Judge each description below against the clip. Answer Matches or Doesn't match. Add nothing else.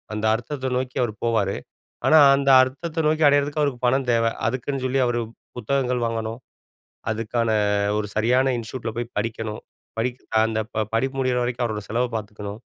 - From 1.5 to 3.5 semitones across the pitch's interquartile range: Matches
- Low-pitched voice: Matches